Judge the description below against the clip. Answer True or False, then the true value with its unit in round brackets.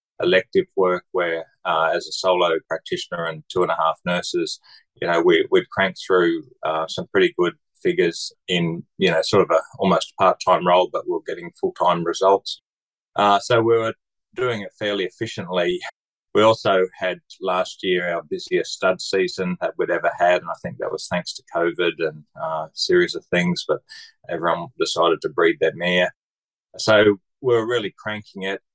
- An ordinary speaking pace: True (190 wpm)